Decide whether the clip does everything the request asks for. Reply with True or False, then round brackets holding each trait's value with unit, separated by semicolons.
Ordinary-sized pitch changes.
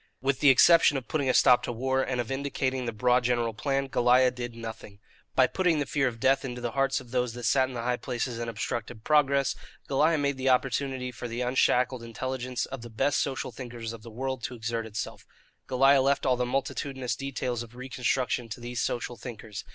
False (2.1 semitones)